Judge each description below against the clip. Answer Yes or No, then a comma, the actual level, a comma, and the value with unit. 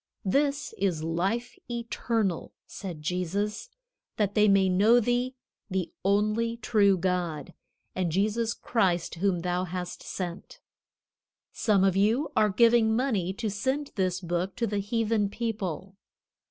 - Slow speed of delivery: Yes, slow, 130 wpm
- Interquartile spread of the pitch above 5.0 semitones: No, average, 4.0 semitones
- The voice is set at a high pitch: Yes, high, 200 Hz